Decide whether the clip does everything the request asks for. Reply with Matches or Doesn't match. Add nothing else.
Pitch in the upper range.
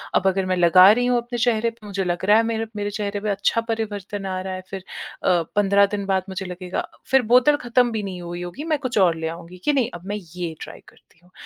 Matches